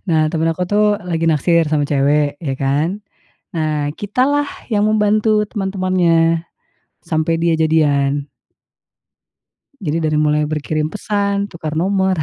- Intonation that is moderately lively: Yes, average, 4.7 semitones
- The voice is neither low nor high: Yes, medium, 165 Hz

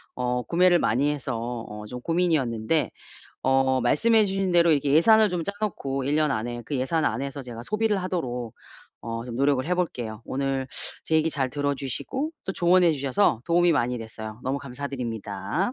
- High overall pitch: No, medium, 140 Hz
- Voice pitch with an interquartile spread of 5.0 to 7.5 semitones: Yes, wide, 5.7 semitones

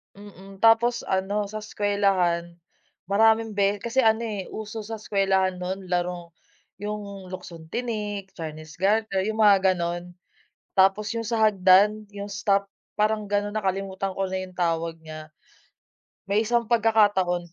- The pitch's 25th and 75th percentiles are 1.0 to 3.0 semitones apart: Yes, narrow, 2.4 semitones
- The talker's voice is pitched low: No, high, 200 Hz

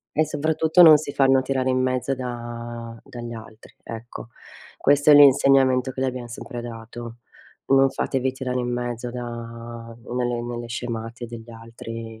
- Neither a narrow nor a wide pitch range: No, narrow, 2.1 semitones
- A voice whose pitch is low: Yes, low, 120 Hz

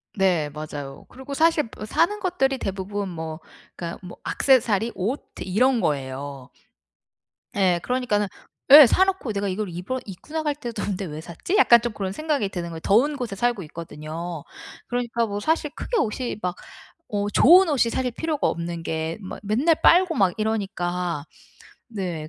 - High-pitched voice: Yes, high, 205 Hz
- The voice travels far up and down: Yes, wide, 7.0 semitones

